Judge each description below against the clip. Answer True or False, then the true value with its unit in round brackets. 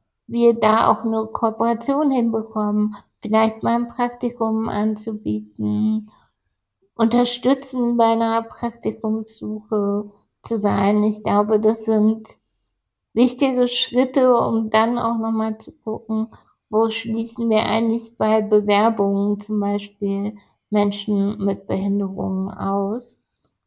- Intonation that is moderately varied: False (1.9 semitones)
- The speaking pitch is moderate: False (220 Hz)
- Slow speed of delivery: True (105 wpm)